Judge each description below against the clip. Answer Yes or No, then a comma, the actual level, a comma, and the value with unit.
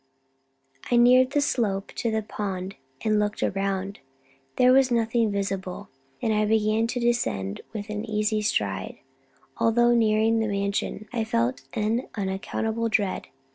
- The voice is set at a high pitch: Yes, high, 215 Hz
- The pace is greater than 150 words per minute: No, average, 140 wpm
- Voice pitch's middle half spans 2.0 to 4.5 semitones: Yes, narrow, 2.6 semitones